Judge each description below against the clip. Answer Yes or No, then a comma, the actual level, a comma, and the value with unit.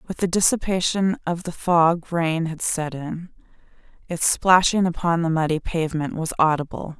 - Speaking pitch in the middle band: Yes, medium, 170 Hz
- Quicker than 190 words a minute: No, average, 155 wpm